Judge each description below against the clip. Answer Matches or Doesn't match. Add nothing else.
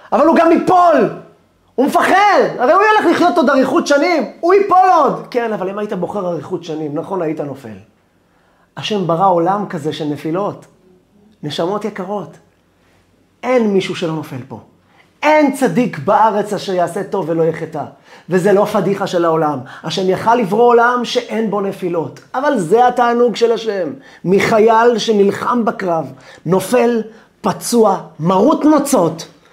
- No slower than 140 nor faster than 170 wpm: Matches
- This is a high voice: Matches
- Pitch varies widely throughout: Matches